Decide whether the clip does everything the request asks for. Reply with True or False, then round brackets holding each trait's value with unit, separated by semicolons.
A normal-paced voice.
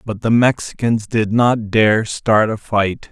True (175 wpm)